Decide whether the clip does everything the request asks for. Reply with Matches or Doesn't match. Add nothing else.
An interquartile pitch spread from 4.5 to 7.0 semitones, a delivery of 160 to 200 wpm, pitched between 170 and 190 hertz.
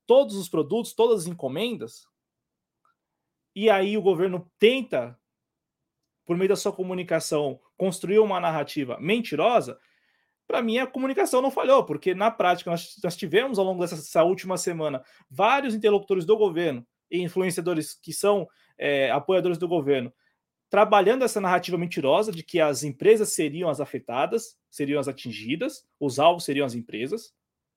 Doesn't match